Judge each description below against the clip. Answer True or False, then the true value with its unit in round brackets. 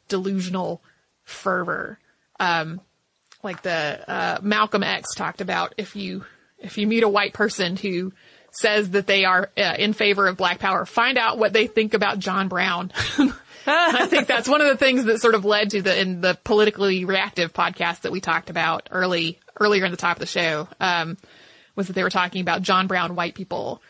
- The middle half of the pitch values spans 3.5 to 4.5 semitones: False (2.7 semitones)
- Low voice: False (195 Hz)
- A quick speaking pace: False (195 wpm)